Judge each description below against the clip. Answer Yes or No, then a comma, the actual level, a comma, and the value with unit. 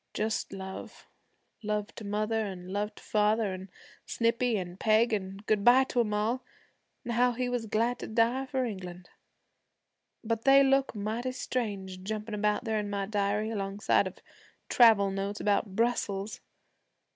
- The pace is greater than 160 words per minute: No, average, 155 wpm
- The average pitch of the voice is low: No, high, 215 Hz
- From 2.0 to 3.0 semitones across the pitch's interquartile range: Yes, narrow, 2.6 semitones